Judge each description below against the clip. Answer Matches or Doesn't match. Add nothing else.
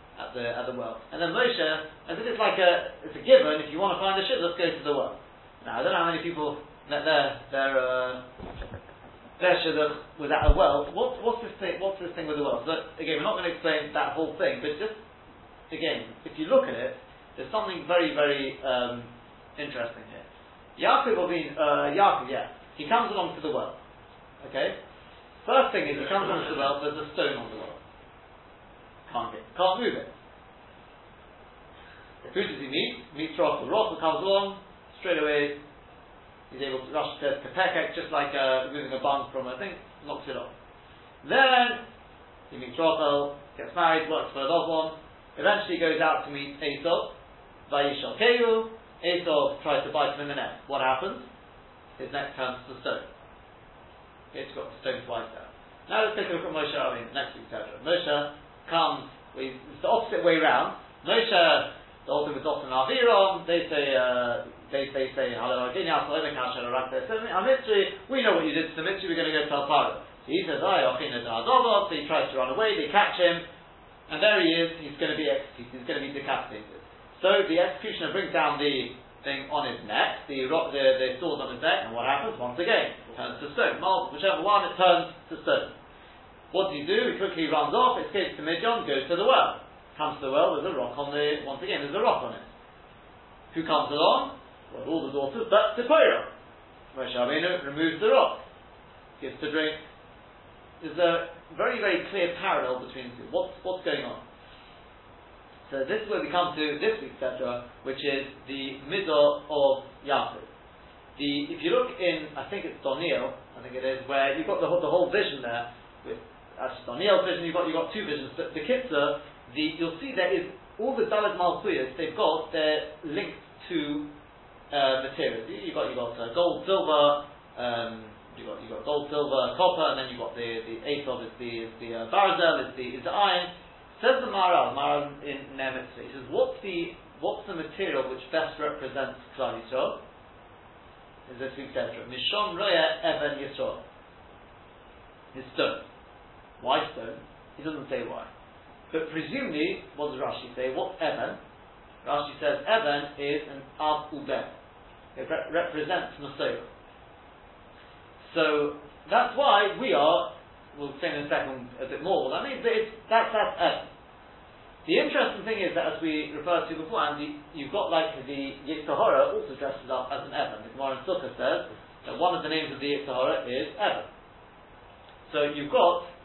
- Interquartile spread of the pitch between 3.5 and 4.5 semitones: Doesn't match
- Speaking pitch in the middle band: Matches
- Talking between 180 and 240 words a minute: Matches